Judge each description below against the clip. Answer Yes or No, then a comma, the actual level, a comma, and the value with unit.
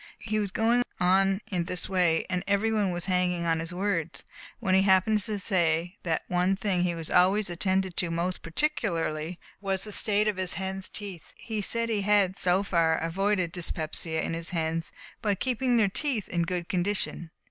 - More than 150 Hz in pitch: Yes, medium, 185 Hz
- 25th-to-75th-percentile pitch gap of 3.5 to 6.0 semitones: No, average, 3.0 semitones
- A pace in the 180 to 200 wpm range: Yes, average, 185 wpm